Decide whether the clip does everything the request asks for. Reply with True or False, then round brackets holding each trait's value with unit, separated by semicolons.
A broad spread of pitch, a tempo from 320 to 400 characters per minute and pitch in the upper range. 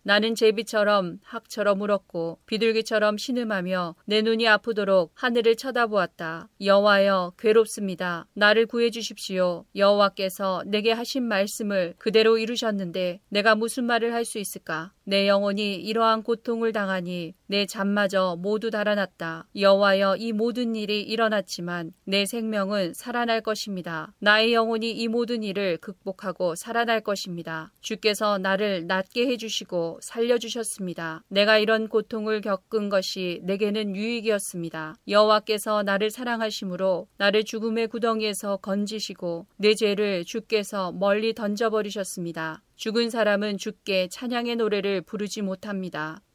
False (2.7 semitones; 330 characters per minute; 205 Hz)